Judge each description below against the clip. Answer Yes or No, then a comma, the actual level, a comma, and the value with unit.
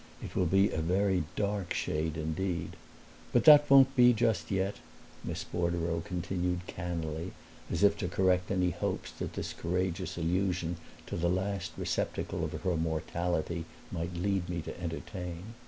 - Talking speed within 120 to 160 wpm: Yes, average, 155 wpm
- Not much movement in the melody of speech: Yes, narrow, 2.3 semitones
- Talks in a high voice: No, very low, 90 Hz